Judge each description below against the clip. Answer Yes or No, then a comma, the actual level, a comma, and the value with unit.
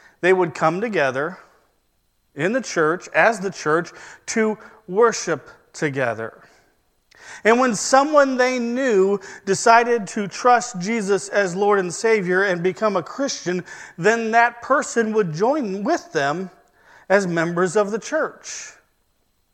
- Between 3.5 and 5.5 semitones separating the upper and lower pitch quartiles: Yes, average, 4.3 semitones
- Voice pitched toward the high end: Yes, high, 215 Hz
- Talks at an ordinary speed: No, slow, 130 wpm